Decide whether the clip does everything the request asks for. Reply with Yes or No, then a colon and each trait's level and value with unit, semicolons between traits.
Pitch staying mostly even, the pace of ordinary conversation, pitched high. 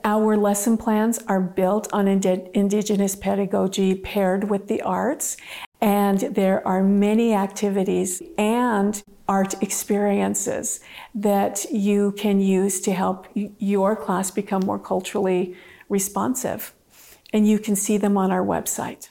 No: narrow, 1.5 semitones; slow, 130 wpm; high, 200 Hz